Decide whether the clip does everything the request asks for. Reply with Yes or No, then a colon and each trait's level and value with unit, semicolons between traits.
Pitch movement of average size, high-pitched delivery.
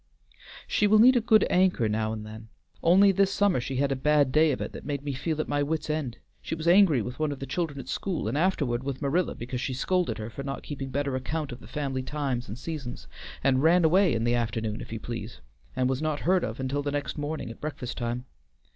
No: average, 4.4 semitones; medium, 140 Hz